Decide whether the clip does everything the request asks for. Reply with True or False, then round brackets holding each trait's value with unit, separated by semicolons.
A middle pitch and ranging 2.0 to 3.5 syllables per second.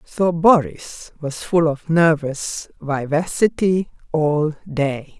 True (160 Hz; 3.1 syllables/s)